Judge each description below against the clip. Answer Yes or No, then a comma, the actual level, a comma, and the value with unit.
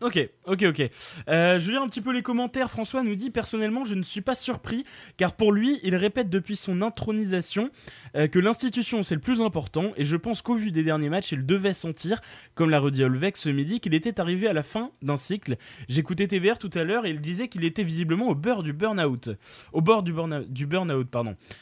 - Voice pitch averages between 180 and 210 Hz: Yes, medium, 185 Hz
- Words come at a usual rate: No, fast, 230 wpm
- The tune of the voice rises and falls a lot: Yes, wide, 6.4 semitones